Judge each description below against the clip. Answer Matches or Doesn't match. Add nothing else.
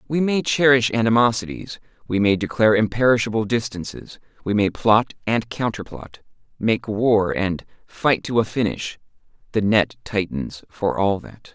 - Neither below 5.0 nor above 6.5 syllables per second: Doesn't match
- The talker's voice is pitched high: Doesn't match